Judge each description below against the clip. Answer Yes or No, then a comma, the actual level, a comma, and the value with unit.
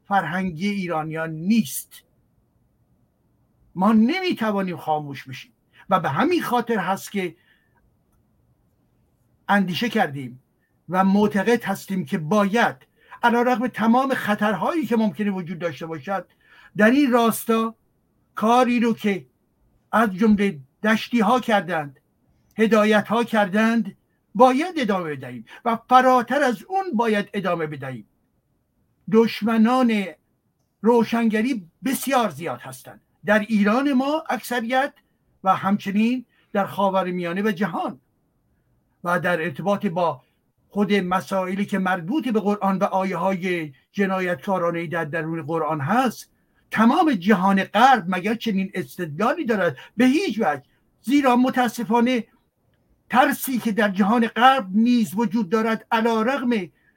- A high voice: Yes, high, 210 Hz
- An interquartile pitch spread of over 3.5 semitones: Yes, average, 4.7 semitones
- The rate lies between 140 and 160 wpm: No, average, 115 wpm